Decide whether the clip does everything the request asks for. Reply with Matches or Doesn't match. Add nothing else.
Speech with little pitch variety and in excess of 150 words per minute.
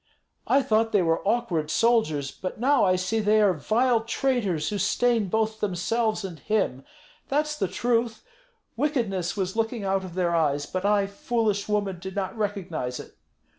Doesn't match